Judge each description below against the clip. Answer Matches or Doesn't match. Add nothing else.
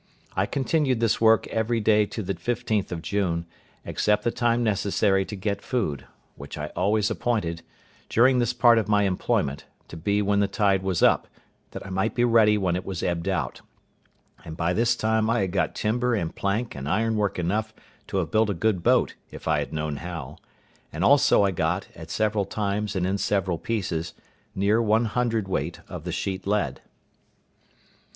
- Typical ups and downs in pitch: Matches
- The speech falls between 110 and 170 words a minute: Doesn't match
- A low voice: Matches